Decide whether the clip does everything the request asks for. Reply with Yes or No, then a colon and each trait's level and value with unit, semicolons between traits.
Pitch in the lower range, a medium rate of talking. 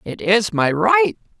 No: medium, 165 Hz; average, 170 wpm